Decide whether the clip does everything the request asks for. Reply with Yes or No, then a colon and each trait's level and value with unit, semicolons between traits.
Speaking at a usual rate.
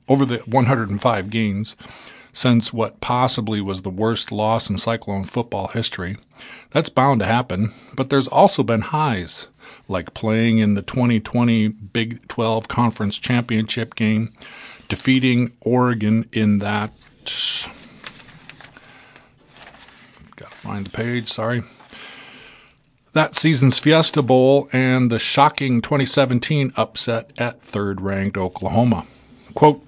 No: slow, 115 wpm